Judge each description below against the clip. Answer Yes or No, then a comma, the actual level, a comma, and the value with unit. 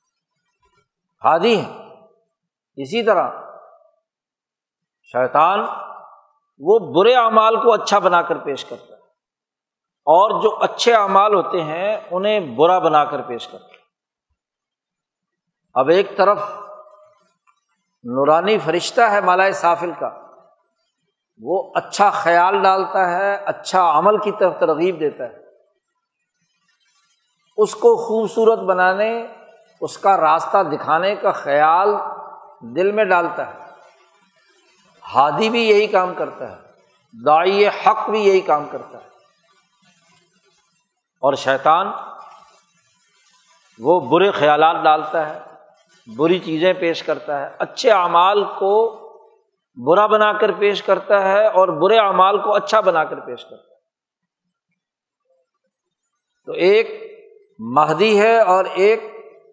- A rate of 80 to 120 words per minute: Yes, average, 115 wpm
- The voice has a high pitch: Yes, high, 200 Hz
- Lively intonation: No, average, 4.4 semitones